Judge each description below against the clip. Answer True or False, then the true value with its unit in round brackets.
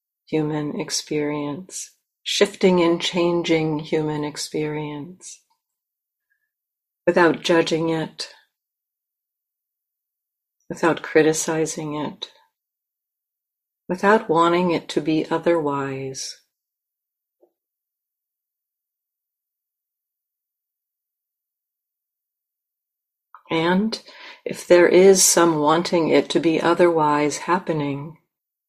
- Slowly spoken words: True (65 wpm)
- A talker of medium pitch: True (165 Hz)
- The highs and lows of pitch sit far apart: False (2.7 semitones)